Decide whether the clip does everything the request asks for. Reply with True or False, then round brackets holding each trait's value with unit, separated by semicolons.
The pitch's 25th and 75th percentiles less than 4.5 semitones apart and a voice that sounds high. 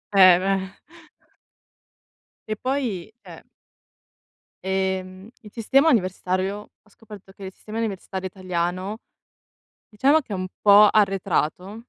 True (2.5 semitones; 195 Hz)